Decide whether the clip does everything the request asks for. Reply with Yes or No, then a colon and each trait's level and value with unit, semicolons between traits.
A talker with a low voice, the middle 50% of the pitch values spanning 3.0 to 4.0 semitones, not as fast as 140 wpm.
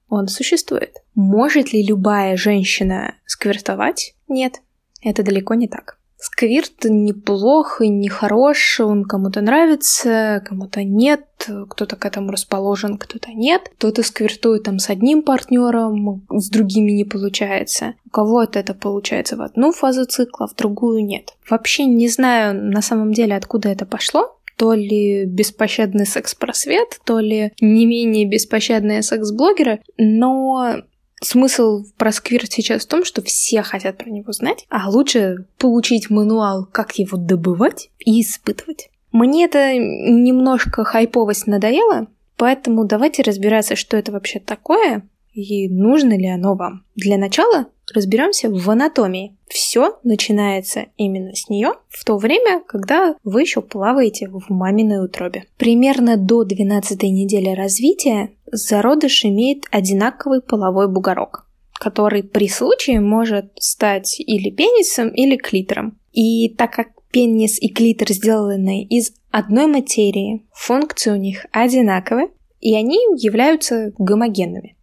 No: high, 220 Hz; average, 3.5 semitones; average, 130 wpm